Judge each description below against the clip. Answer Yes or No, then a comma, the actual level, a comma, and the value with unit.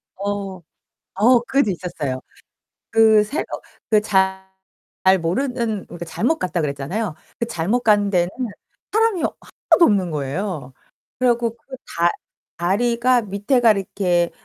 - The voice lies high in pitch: Yes, high, 200 Hz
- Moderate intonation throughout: Yes, average, 4.9 semitones